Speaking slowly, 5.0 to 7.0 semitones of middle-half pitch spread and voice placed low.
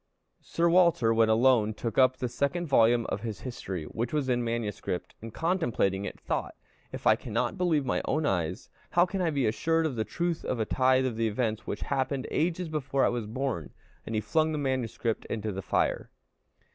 No: average, 200 wpm; wide, 5.5 semitones; low, 130 Hz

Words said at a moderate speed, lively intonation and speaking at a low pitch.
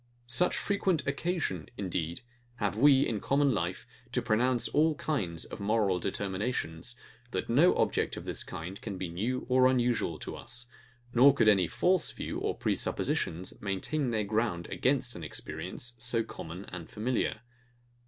Yes: average, 155 wpm; wide, 5.7 semitones; low, 115 Hz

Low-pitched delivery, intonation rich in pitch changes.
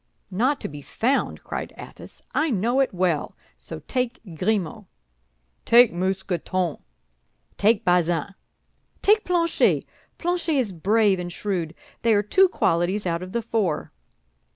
No: high, 200 Hz; wide, 5.7 semitones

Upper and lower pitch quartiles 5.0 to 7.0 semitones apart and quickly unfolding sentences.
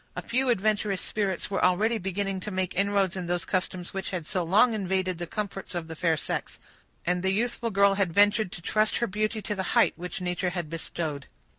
No: average, 2.7 semitones; fast, 210 wpm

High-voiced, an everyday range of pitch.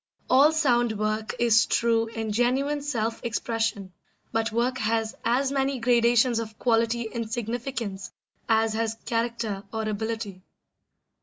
No: high, 230 Hz; narrow, 1.6 semitones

